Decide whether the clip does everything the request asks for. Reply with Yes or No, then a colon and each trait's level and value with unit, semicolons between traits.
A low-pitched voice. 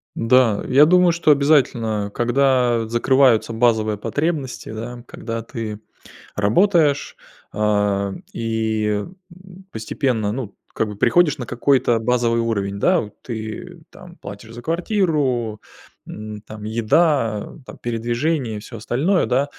Yes: low, 120 Hz